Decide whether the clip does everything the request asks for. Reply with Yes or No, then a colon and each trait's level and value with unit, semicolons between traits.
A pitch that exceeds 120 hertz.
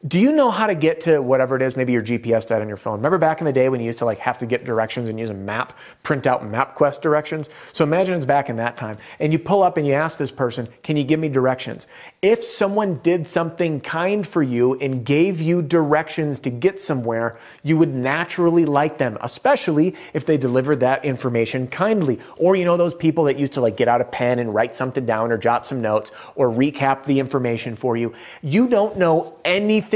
Yes: medium, 140 Hz